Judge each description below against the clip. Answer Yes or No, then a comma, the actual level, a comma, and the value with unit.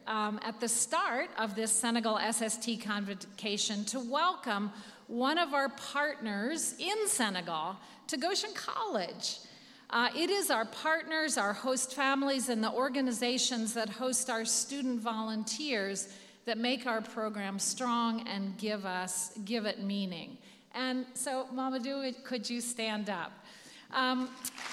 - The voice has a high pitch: Yes, high, 235 Hz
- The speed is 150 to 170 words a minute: No, slow, 135 wpm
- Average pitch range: Yes, average, 3.5 semitones